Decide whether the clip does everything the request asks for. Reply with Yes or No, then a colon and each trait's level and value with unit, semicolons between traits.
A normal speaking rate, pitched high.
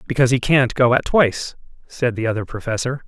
No: average, 195 wpm; low, 125 Hz